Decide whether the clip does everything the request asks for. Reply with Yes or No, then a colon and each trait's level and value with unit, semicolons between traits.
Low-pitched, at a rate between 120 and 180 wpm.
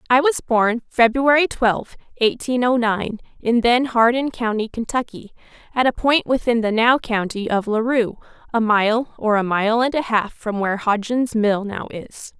No: high, 230 Hz; average, 175 wpm